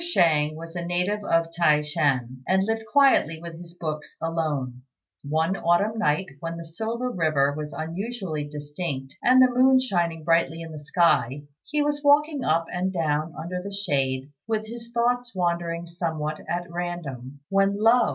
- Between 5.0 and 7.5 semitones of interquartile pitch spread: Yes, average, 5.3 semitones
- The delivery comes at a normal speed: Yes, average, 165 wpm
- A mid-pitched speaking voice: Yes, medium, 170 Hz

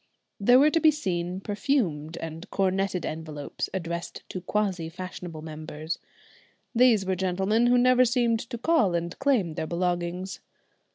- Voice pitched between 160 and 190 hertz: Yes, medium, 185 Hz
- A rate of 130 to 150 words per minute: Yes, average, 145 wpm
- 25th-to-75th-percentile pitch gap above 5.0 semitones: Yes, wide, 5.6 semitones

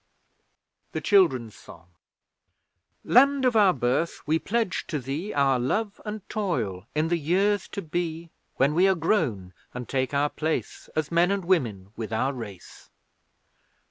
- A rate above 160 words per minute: No, average, 150 wpm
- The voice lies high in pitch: No, medium, 160 Hz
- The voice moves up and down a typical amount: No, wide, 7.3 semitones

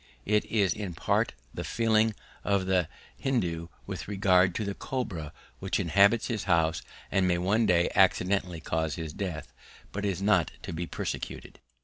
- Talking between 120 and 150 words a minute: No, average, 160 wpm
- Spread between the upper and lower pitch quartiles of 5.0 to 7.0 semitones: No, average, 3.3 semitones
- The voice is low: Yes, very low, 95 Hz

